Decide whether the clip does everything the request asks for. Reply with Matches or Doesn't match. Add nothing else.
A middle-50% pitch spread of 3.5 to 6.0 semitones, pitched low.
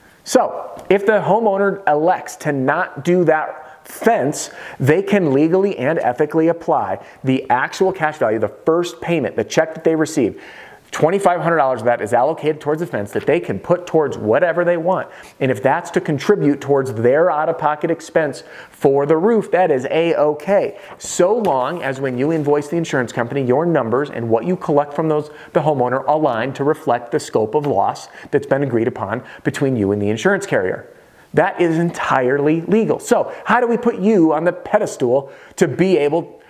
Doesn't match